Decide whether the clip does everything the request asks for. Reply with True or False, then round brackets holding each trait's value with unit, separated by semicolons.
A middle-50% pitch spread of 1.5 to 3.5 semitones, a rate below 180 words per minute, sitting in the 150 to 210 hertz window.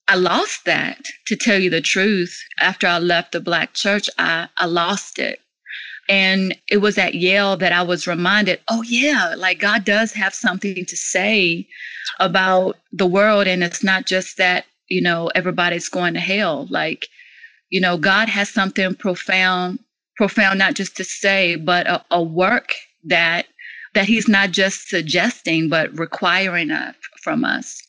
True (2.6 semitones; 165 wpm; 190 Hz)